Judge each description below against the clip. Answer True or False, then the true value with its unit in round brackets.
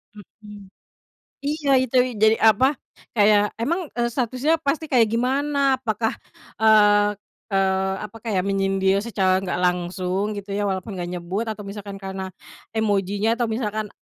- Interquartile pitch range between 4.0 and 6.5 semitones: False (3.2 semitones)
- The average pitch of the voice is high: True (210 Hz)